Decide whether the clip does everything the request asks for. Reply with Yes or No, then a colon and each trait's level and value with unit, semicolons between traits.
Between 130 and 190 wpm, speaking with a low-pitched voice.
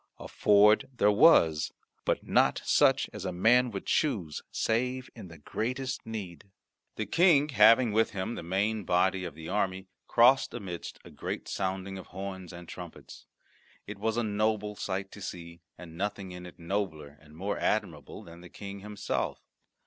Yes: average, 170 wpm; low, 100 Hz